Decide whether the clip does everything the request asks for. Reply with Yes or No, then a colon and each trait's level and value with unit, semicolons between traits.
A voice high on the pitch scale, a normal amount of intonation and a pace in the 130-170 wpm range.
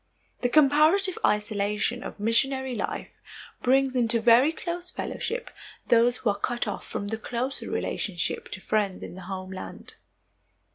Yes: high, 235 Hz; average, 4.6 semitones; average, 140 wpm